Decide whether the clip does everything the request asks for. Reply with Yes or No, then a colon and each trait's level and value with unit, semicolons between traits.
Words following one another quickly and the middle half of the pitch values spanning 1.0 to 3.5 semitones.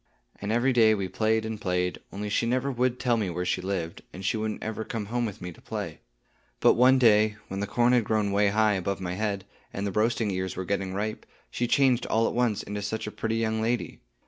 Yes: fast, 240 wpm; average, 2.7 semitones